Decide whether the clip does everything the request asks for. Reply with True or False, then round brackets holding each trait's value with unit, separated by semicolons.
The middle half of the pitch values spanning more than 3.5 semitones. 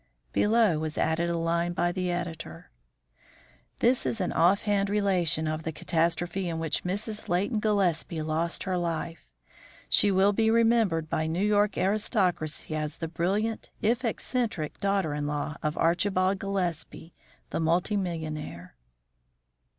True (4.0 semitones)